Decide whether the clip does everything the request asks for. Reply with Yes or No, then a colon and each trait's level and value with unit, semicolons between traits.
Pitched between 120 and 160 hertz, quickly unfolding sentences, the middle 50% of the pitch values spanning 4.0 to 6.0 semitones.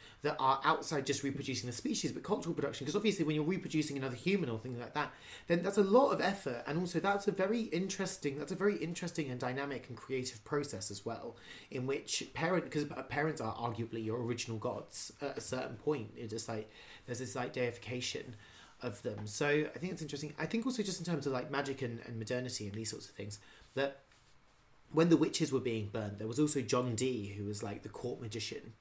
Yes: low, 135 Hz; fast, 225 wpm; wide, 5.4 semitones